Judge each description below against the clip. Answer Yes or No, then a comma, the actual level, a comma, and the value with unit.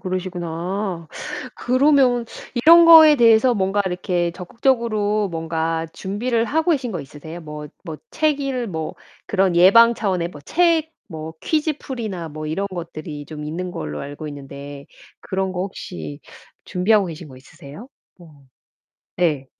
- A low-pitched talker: No, medium, 185 Hz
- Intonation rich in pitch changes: Yes, wide, 6.6 semitones